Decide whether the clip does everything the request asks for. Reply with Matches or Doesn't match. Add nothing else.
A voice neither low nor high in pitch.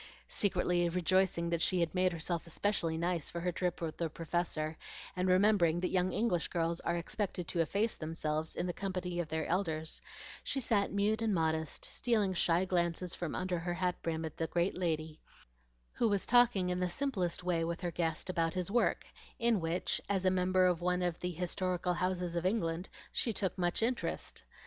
Matches